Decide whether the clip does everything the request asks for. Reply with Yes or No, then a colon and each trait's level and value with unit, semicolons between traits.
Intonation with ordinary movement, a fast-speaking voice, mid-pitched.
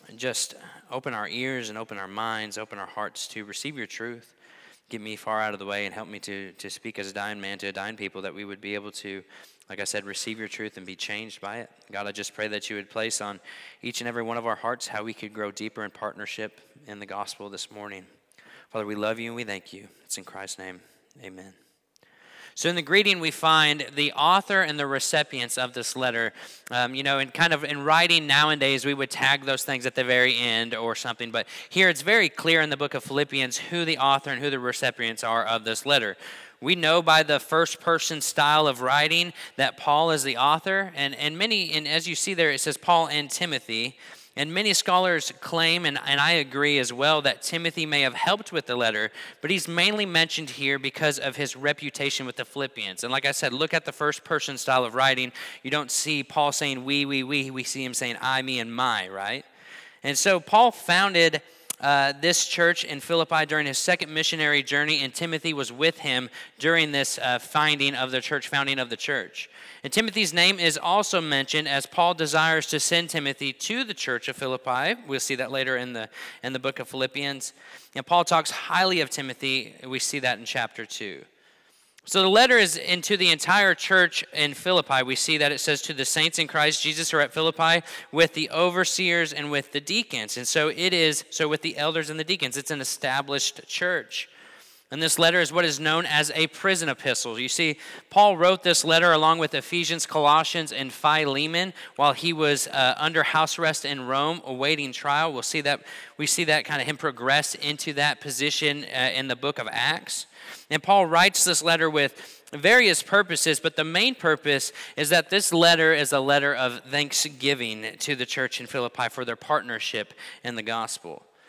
Yes: average, 4.4 semitones; fast, 215 wpm; medium, 145 Hz